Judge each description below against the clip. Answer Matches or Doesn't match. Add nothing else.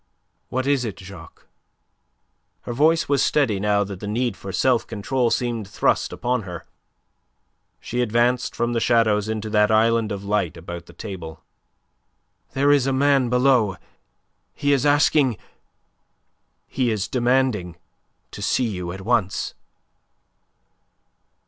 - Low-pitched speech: Matches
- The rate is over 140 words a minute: Doesn't match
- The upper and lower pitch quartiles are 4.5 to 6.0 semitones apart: Doesn't match